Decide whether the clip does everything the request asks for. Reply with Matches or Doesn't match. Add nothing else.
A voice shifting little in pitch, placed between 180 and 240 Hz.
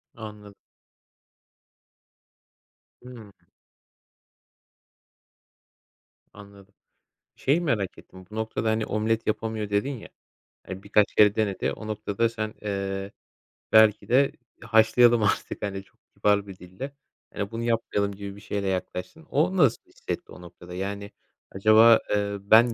Doesn't match